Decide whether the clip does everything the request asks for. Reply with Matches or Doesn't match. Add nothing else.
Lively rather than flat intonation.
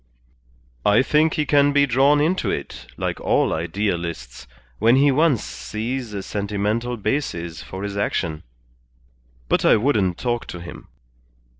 Matches